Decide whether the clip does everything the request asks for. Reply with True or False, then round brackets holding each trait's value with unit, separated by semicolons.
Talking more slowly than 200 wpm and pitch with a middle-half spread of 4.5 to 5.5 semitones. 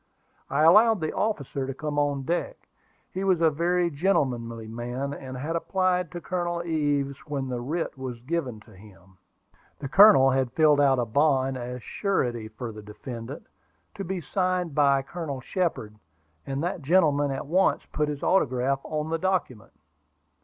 True (165 wpm; 5.1 semitones)